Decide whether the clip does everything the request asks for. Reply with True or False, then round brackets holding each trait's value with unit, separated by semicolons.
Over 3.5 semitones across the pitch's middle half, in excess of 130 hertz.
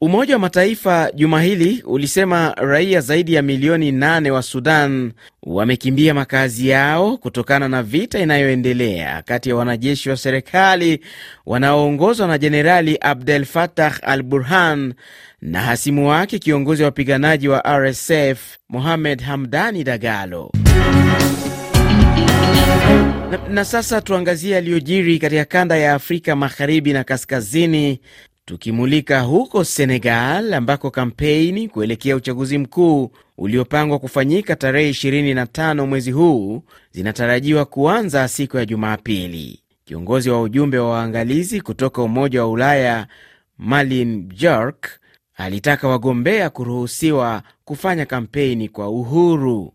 True (4.1 semitones; 140 Hz)